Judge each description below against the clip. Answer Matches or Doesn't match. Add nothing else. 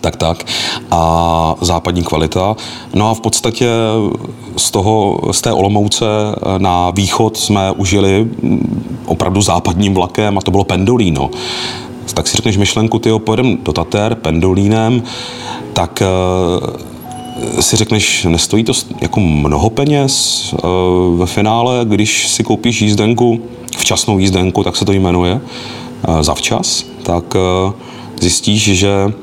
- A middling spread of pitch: Matches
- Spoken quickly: Doesn't match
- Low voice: Matches